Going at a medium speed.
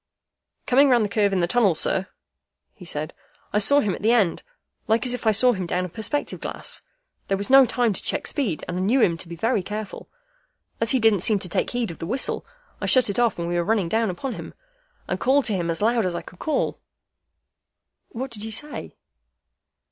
No: fast, 230 wpm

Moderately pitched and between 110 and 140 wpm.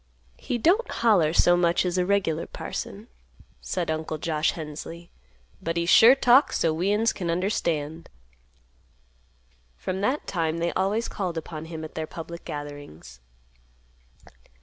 Yes: medium, 170 Hz; slow, 135 wpm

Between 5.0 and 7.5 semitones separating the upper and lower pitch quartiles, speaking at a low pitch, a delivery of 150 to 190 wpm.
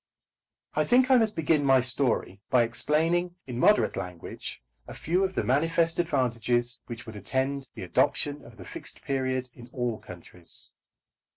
Yes: wide, 5.4 semitones; low, 130 Hz; average, 160 wpm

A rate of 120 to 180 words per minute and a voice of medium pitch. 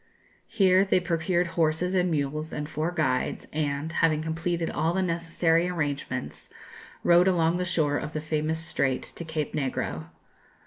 Yes: average, 150 wpm; medium, 160 Hz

